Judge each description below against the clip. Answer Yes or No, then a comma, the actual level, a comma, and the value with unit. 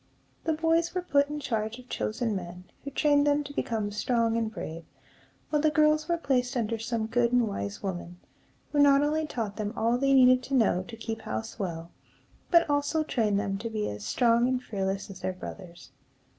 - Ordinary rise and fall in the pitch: No, wide, 5.7 semitones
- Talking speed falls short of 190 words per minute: No, average, 200 wpm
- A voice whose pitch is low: No, high, 235 Hz